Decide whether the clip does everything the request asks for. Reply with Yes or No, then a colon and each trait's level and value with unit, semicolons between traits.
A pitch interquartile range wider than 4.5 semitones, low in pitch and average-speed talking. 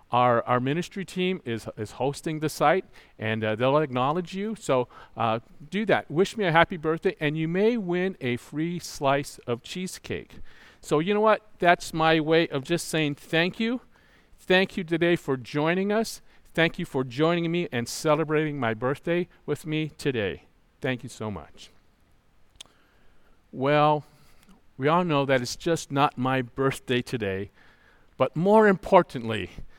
No: average, 5.2 semitones; medium, 155 Hz; average, 160 wpm